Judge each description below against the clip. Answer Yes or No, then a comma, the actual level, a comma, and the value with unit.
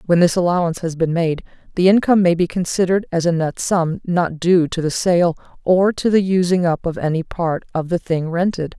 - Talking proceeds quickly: Yes, fast, 220 wpm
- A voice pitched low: No, medium, 175 Hz